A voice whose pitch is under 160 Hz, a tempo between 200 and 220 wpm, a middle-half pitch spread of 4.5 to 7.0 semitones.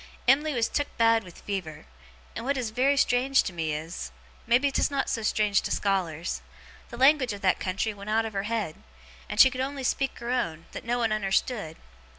No: high, 225 Hz; fast, 205 wpm; average, 4.8 semitones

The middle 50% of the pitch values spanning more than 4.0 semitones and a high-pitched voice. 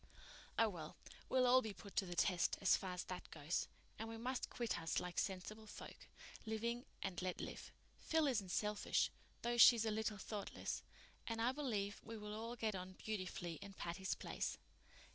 No: average, 3.6 semitones; high, 210 Hz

